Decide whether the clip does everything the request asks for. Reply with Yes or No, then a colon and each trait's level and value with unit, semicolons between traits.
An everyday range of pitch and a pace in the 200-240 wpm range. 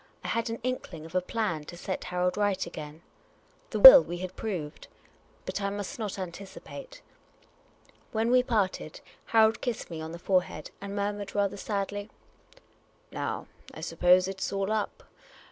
No: average, 3.4 semitones; average, 165 wpm